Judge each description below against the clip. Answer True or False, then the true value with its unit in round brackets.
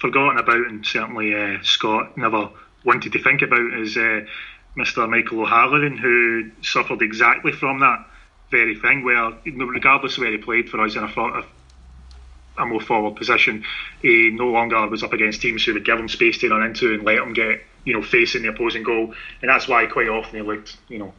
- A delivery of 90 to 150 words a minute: False (200 wpm)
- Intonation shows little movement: True (2.2 semitones)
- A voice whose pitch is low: True (115 Hz)